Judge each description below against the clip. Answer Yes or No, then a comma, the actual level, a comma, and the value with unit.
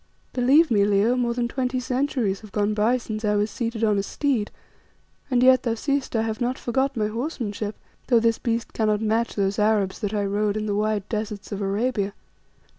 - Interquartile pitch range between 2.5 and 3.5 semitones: Yes, average, 3.0 semitones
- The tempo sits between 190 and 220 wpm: Yes, average, 200 wpm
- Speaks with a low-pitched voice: No, high, 220 Hz